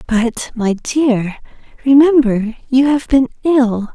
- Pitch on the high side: Yes, very high, 250 Hz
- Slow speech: Yes, slow, 120 wpm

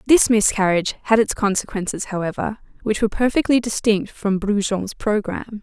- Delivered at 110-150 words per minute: Yes, average, 140 wpm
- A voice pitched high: Yes, high, 210 Hz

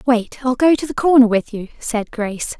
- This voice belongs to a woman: Yes, female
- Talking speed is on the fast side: Yes, fast, 230 wpm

